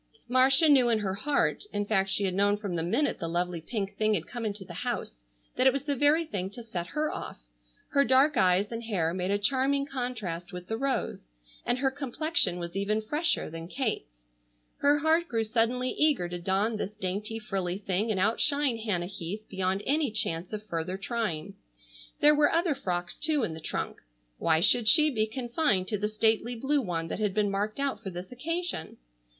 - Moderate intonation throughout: No, wide, 6.1 semitones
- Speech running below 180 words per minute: No, average, 200 wpm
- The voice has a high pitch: Yes, high, 215 Hz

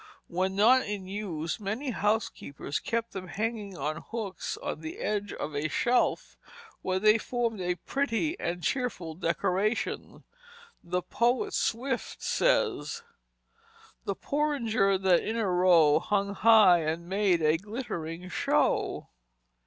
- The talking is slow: Yes, slow, 130 wpm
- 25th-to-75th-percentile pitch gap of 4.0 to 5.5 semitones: Yes, average, 4.5 semitones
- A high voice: Yes, high, 200 Hz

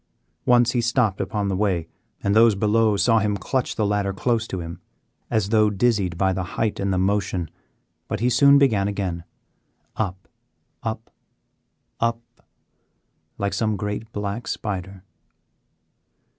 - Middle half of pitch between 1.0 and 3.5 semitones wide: Yes, average, 2.7 semitones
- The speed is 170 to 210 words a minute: No, average, 145 wpm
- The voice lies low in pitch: Yes, low, 105 Hz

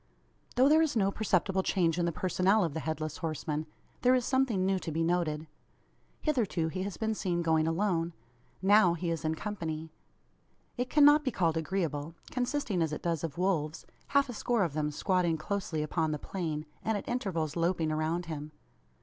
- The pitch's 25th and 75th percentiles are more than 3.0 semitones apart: Yes, average, 4.4 semitones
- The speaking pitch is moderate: Yes, medium, 175 Hz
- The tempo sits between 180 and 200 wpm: Yes, average, 185 wpm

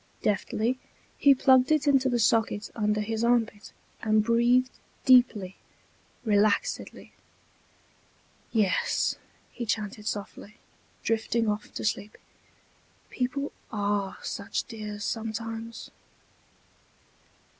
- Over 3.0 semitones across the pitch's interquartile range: No, narrow, 2.6 semitones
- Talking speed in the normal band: No, slow, 90 wpm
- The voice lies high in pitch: Yes, high, 225 Hz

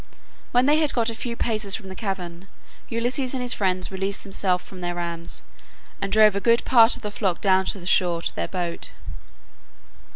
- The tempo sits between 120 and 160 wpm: No, average, 200 wpm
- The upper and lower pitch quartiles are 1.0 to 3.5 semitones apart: No, average, 4.1 semitones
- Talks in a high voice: Yes, high, 195 Hz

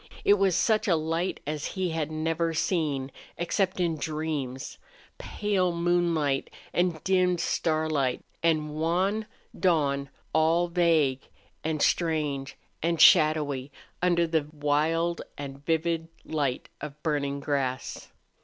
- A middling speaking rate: No, slow, 115 wpm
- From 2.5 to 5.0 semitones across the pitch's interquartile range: Yes, average, 2.8 semitones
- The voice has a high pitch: No, medium, 160 Hz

